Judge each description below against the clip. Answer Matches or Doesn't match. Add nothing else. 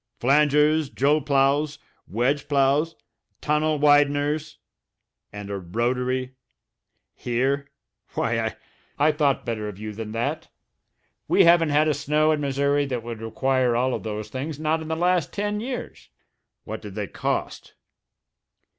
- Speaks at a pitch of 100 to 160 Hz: Matches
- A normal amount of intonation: Matches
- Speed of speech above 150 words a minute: Doesn't match